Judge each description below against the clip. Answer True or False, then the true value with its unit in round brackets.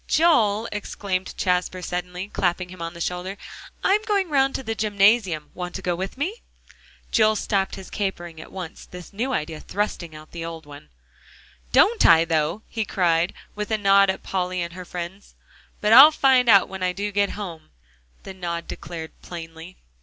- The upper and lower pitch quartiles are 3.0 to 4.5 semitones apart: True (3.5 semitones)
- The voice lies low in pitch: False (190 Hz)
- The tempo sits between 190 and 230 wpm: False (180 wpm)